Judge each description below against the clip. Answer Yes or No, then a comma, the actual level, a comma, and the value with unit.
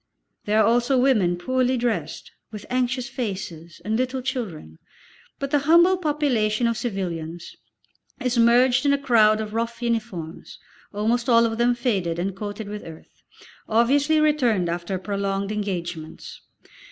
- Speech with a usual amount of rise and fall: Yes, average, 4.5 semitones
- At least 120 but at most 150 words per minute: Yes, average, 140 wpm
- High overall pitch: Yes, high, 230 Hz